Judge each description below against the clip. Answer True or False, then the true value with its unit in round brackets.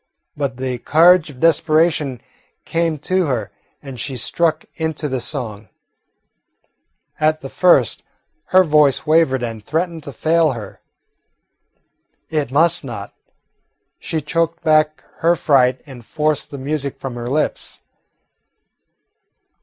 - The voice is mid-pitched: True (150 Hz)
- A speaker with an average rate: False (120 wpm)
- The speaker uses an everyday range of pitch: True (3.7 semitones)